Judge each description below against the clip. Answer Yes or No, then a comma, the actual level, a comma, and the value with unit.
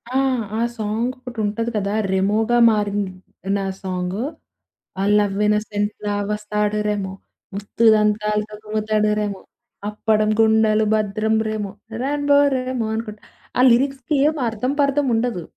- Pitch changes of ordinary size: No, narrow, 1.9 semitones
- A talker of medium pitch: No, high, 215 Hz